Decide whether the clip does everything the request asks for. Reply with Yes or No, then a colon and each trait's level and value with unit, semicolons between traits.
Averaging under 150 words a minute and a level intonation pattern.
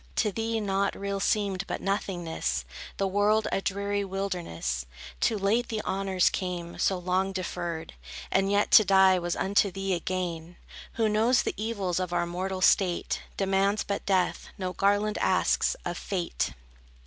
No: average, 160 wpm; narrow, 2.0 semitones